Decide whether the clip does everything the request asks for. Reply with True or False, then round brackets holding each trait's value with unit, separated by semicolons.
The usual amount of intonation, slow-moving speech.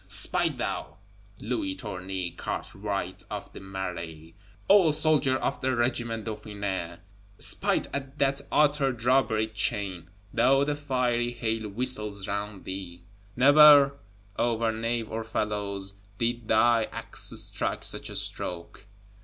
True (4.9 semitones; 120 wpm)